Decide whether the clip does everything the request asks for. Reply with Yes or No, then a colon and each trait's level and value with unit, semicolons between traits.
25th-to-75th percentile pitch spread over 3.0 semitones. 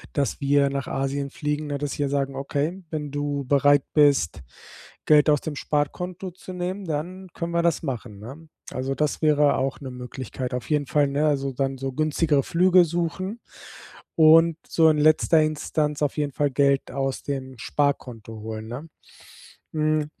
No: narrow, 2.4 semitones